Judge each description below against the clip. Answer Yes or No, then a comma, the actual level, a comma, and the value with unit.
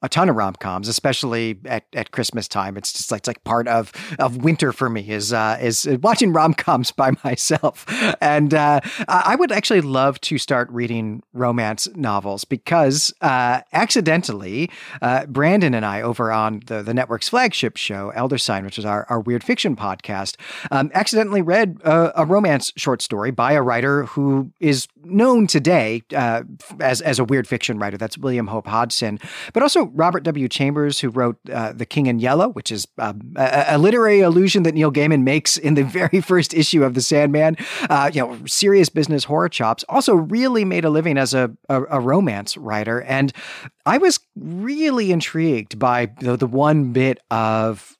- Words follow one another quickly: No, average, 185 wpm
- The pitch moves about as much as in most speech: No, wide, 6.1 semitones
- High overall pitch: No, low, 135 Hz